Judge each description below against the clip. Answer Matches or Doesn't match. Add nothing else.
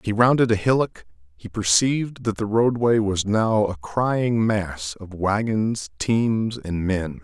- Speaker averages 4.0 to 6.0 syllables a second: Doesn't match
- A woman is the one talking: Doesn't match